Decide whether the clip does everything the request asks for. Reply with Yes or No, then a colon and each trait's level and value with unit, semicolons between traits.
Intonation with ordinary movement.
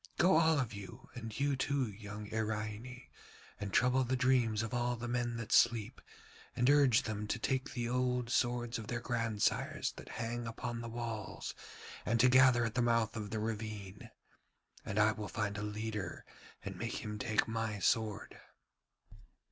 No: narrow, 2.3 semitones